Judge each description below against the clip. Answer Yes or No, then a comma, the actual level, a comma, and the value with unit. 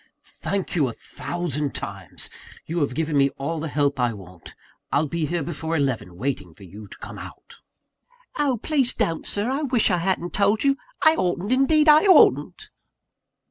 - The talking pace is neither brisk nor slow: Yes, average, 180 wpm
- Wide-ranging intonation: Yes, wide, 7.4 semitones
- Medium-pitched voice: Yes, medium, 165 Hz